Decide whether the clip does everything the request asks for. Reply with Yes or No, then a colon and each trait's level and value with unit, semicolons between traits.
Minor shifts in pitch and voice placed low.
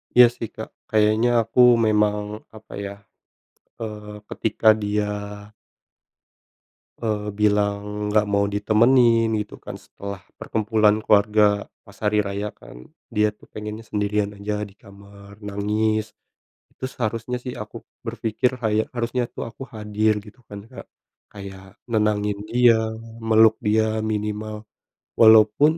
Yes: narrow, 1.3 semitones; low, 105 Hz